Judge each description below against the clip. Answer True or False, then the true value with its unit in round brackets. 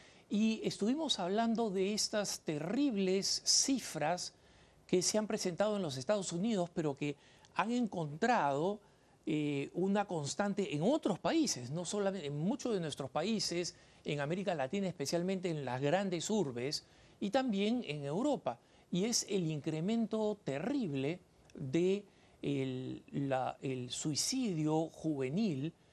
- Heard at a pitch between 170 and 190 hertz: True (185 Hz)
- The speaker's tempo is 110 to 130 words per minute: True (125 wpm)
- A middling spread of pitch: False (5.8 semitones)